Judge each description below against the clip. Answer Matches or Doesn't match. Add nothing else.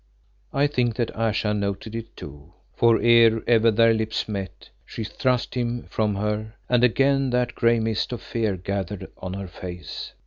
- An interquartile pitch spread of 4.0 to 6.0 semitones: Doesn't match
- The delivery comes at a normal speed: Matches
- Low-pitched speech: Matches